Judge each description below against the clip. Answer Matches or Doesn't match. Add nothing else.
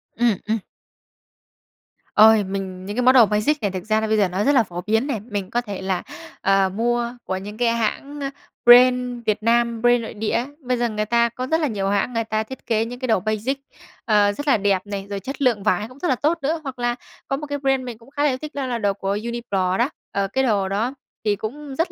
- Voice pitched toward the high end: Matches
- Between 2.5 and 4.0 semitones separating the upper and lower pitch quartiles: Matches